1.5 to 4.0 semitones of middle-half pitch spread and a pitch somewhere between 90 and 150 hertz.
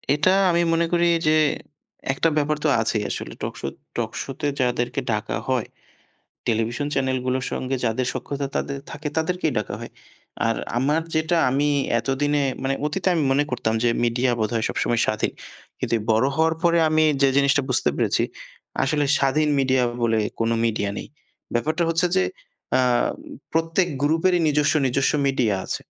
No: average, 4.4 semitones; low, 135 Hz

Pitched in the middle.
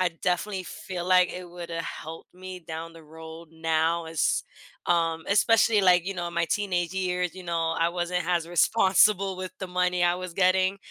Yes: medium, 180 Hz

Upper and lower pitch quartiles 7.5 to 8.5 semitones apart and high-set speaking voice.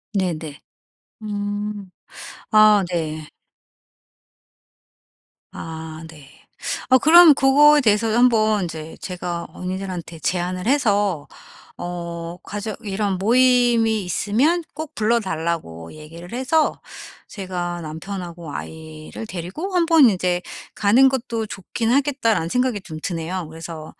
No: wide, 5.6 semitones; high, 195 Hz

